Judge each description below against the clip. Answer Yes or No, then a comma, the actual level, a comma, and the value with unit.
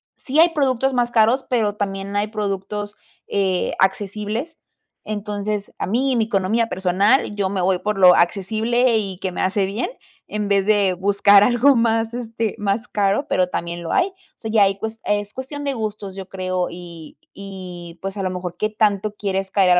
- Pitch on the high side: Yes, high, 205 Hz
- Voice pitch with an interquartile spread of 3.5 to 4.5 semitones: No, average, 2.8 semitones